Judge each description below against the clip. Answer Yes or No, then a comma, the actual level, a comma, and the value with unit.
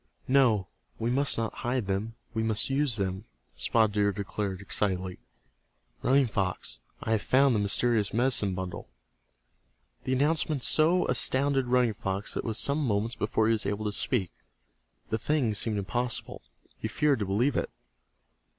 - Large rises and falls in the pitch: No, average, 4.2 semitones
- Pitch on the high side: No, low, 110 Hz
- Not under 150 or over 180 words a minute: Yes, average, 160 wpm